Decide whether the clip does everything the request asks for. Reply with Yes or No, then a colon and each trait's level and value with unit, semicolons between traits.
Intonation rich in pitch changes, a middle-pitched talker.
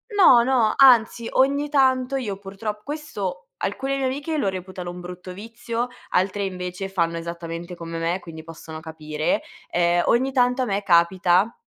No: wide, 6.3 semitones; high, 195 Hz